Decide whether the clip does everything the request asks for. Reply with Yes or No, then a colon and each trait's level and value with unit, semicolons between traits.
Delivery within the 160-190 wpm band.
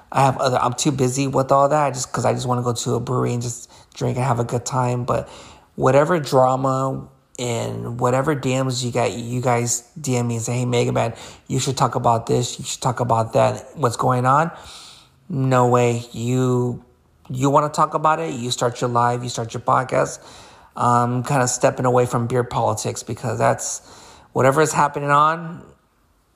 No: average, 200 wpm